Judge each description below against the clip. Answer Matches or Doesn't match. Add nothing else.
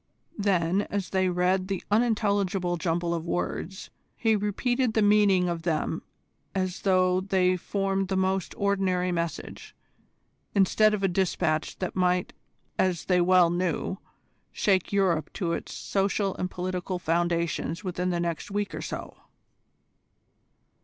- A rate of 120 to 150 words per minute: Matches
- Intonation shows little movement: Matches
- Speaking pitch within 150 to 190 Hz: Matches